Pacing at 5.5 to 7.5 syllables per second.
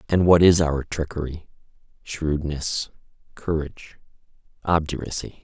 No: 4.4 syllables/s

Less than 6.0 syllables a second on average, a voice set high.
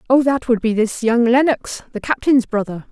Yes: 5.0 syllables/s; high, 240 Hz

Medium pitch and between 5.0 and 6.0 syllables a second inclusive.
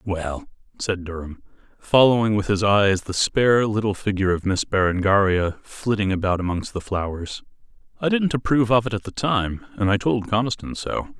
No: low, 100 Hz; 5.2 syllables/s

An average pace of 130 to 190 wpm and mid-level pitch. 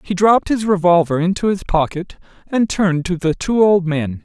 No: average, 200 wpm; medium, 180 Hz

